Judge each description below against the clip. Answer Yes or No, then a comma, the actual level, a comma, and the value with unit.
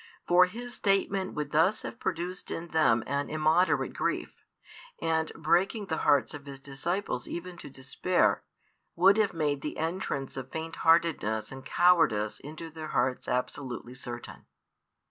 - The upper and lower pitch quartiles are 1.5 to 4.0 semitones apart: No, average, 4.7 semitones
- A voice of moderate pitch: Yes, medium, 160 Hz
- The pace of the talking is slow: No, average, 145 wpm